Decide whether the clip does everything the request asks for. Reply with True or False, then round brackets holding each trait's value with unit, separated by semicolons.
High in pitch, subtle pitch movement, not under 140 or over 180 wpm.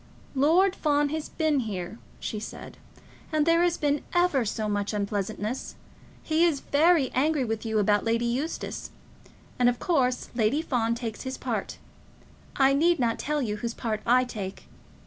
False (255 Hz; 5.5 semitones; 165 wpm)